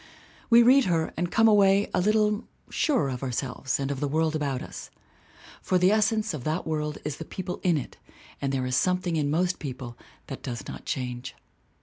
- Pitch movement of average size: No, wide, 6.1 semitones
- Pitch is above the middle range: No, medium, 160 Hz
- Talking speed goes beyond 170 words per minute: Yes, average, 200 wpm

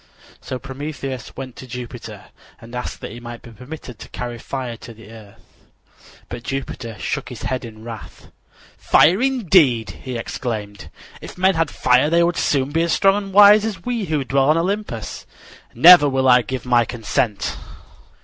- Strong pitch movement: Yes, wide, 5.8 semitones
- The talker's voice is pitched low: Yes, low, 130 Hz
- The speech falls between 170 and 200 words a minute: Yes, average, 175 wpm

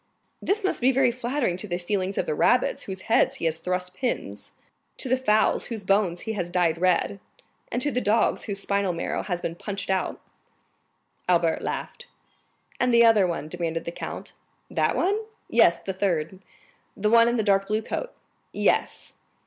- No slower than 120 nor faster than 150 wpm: No, average, 185 wpm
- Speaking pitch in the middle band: No, high, 200 Hz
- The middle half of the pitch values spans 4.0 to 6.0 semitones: Yes, average, 4.7 semitones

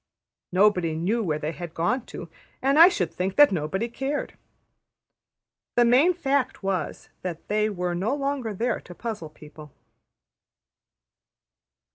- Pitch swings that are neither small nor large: No, wide, 6.7 semitones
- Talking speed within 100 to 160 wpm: Yes, slow, 135 wpm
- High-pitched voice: Yes, high, 205 Hz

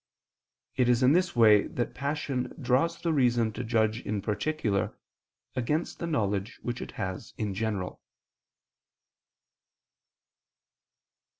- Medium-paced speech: No, slow, 115 wpm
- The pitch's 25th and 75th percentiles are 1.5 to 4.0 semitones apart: No, average, 4.7 semitones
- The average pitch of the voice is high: No, low, 120 Hz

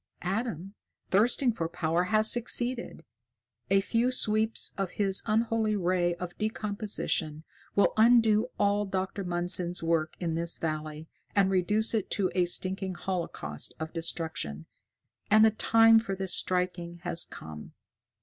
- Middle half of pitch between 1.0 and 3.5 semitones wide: No, average, 4.0 semitones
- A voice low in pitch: No, high, 190 Hz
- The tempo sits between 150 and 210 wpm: No, slow, 135 wpm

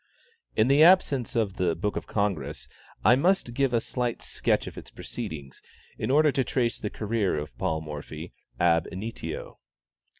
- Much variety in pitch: Yes, wide, 7.3 semitones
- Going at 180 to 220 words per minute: No, average, 170 wpm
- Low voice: Yes, low, 110 Hz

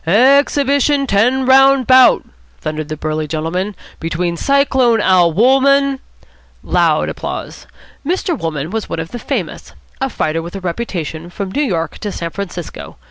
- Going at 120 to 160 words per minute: No, average, 170 wpm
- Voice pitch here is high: Yes, high, 200 Hz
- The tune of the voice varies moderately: No, wide, 8.2 semitones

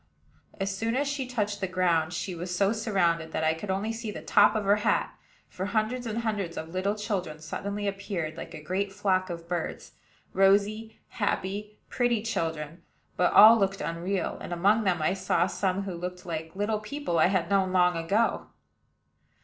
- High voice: Yes, high, 195 Hz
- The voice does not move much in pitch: No, average, 3.2 semitones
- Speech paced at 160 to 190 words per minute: Yes, average, 185 wpm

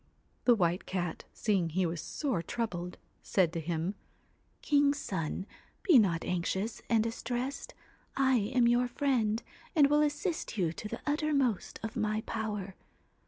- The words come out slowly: No, average, 155 wpm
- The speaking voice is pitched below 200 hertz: No, high, 220 Hz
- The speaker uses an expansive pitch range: Yes, wide, 6.3 semitones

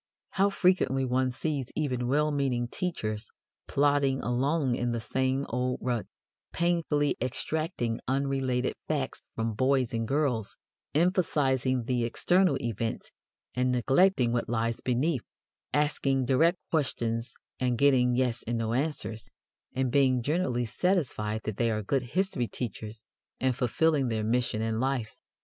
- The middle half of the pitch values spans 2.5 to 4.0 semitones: Yes, average, 3.5 semitones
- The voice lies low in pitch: Yes, low, 130 Hz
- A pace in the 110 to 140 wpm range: Yes, slow, 135 wpm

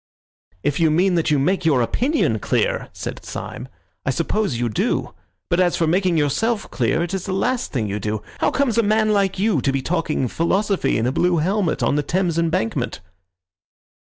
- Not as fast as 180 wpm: No, average, 195 wpm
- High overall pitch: No, medium, 175 Hz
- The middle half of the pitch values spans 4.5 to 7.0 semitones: Yes, wide, 5.5 semitones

